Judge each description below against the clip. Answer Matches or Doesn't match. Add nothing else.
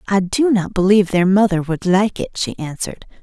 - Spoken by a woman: Matches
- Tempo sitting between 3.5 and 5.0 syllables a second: Doesn't match